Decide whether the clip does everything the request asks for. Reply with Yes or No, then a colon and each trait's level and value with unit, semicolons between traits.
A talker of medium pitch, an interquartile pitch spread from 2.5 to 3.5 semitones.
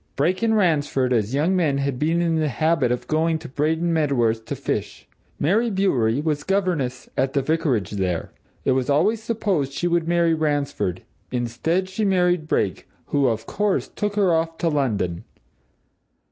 No: medium, 155 Hz; average, 5.1 semitones